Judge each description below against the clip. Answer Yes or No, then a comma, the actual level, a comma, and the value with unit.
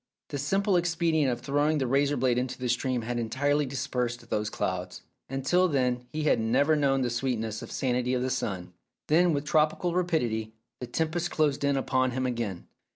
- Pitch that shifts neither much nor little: Yes, average, 3.7 semitones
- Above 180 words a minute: Yes, average, 190 wpm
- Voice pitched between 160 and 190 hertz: No, low, 130 Hz